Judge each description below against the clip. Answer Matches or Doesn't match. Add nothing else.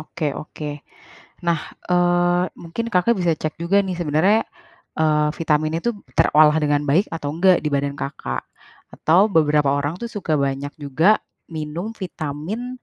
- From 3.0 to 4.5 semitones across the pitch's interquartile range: Matches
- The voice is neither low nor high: Matches